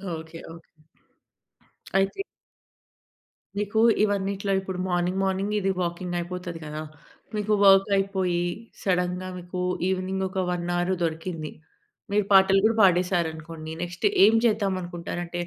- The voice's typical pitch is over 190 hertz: No, medium, 185 Hz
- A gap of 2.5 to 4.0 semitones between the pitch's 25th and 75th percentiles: No, narrow, 1.9 semitones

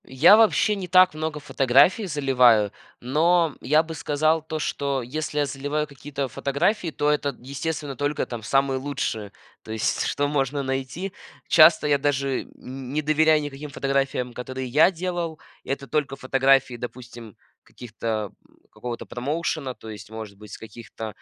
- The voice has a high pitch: No, medium, 140 Hz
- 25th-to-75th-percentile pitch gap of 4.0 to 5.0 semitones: No, average, 3.4 semitones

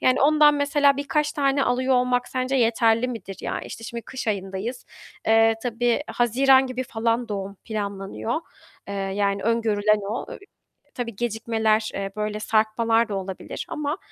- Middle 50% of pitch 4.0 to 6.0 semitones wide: No, average, 3.2 semitones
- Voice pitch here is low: No, high, 230 Hz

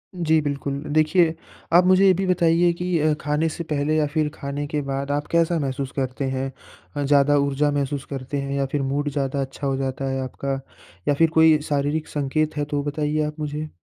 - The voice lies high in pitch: No, medium, 145 Hz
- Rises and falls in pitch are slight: Yes, narrow, 2.1 semitones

